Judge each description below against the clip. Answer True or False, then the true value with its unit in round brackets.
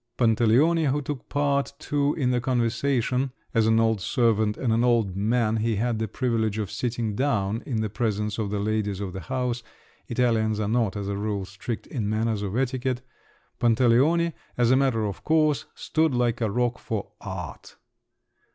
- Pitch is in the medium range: False (115 Hz)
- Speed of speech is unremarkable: True (170 wpm)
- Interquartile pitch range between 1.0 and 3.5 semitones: True (3.0 semitones)